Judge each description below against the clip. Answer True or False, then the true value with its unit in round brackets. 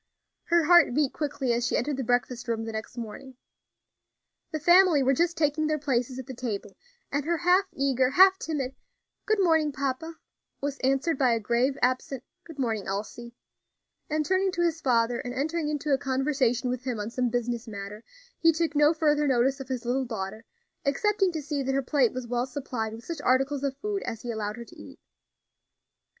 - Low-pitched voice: False (270 Hz)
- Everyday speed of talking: True (195 wpm)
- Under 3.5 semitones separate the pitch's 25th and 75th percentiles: False (4.0 semitones)